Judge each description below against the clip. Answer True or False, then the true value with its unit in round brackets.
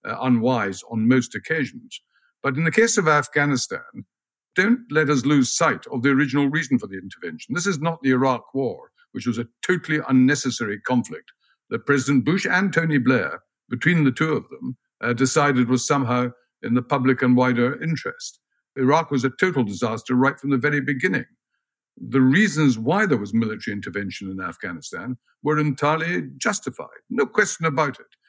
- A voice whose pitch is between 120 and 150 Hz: True (135 Hz)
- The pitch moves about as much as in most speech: True (4.0 semitones)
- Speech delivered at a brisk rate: False (175 wpm)